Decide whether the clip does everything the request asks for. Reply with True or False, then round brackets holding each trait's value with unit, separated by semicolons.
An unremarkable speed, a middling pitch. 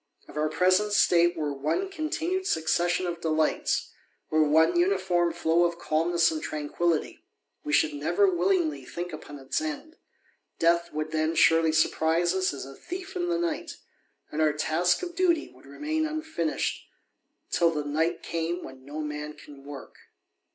True (165 wpm; 170 Hz)